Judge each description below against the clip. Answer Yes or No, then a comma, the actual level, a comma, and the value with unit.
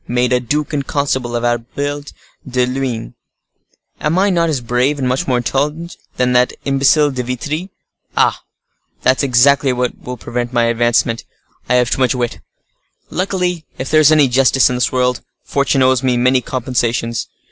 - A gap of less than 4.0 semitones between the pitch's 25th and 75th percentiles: Yes, narrow, 2.6 semitones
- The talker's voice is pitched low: Yes, low, 130 Hz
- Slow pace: No, average, 170 wpm